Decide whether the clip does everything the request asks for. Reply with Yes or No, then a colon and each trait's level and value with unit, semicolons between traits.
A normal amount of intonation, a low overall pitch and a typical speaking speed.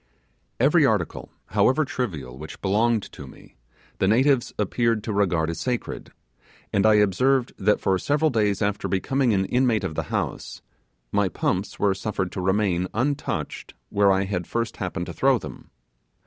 Yes: average, 4.2 semitones; low, 105 Hz; average, 160 wpm